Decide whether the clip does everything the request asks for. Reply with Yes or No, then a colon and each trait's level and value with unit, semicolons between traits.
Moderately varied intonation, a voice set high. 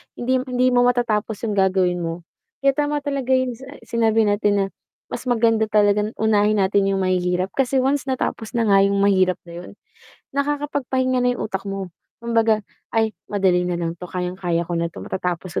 Yes: average, 5.0 semitones; high, 210 Hz